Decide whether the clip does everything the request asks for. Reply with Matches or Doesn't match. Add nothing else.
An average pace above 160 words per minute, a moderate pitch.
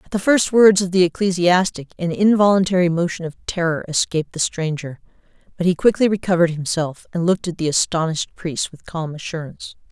Matches